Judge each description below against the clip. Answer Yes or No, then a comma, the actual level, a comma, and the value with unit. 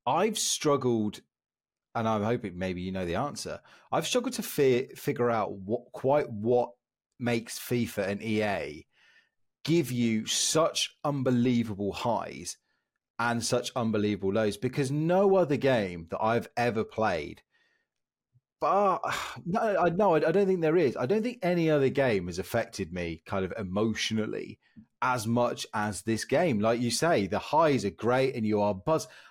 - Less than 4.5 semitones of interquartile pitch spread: No, average, 5.2 semitones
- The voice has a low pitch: Yes, low, 120 Hz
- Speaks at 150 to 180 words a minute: Yes, average, 155 wpm